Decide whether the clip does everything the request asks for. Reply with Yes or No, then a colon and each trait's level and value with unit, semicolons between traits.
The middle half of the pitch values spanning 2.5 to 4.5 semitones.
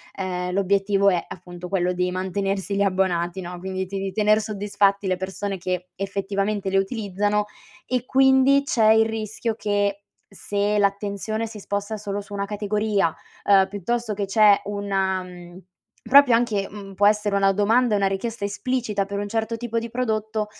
No: narrow, 1.9 semitones